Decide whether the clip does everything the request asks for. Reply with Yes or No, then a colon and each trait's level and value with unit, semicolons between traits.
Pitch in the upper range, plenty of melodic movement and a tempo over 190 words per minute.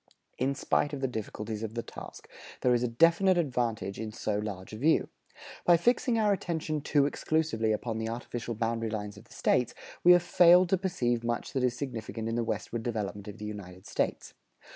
No: low, 120 Hz; wide, 5.7 semitones; average, 200 wpm